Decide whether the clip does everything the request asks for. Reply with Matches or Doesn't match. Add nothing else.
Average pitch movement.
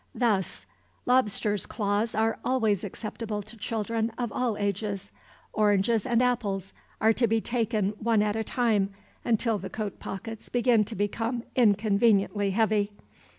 Doesn't match